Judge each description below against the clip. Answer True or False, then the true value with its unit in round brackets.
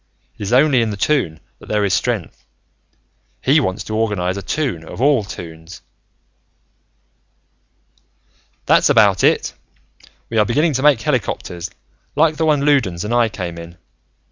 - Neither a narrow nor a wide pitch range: False (7.3 semitones)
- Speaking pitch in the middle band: False (110 Hz)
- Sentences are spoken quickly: False (150 wpm)